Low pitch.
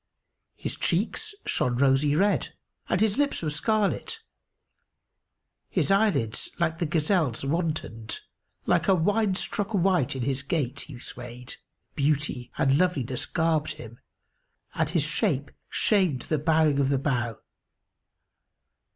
No: medium, 155 Hz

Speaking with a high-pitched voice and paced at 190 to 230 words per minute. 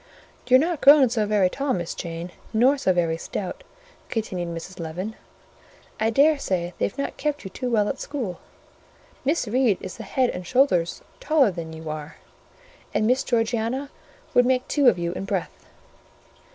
No: high, 220 Hz; average, 170 wpm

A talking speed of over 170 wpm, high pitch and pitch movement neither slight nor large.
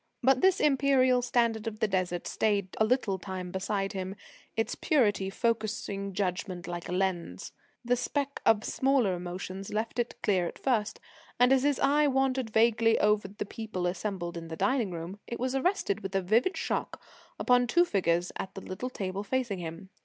Yes: average, 180 wpm; high, 210 Hz; average, 4.9 semitones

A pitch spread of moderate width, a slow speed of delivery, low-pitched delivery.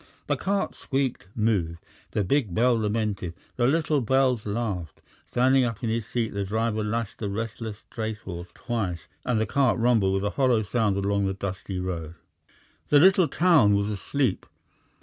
No: average, 3.8 semitones; average, 165 wpm; low, 110 Hz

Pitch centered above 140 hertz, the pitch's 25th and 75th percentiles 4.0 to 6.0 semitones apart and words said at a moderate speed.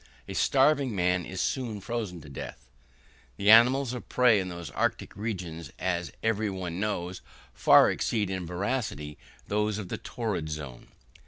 No: low, 100 Hz; average, 4.5 semitones; average, 155 wpm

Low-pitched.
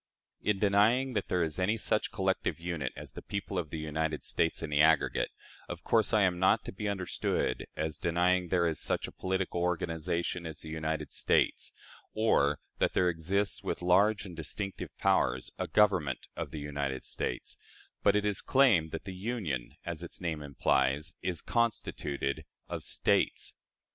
Yes: very low, 90 Hz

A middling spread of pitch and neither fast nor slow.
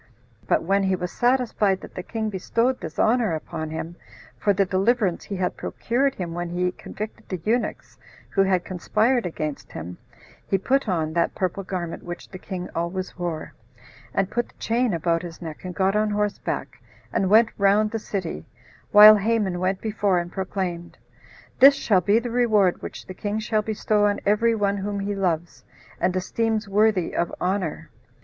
Yes: average, 3.3 semitones; average, 180 wpm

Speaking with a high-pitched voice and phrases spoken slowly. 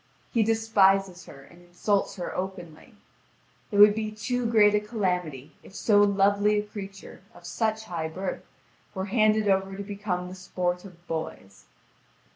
No: high, 195 Hz; average, 155 wpm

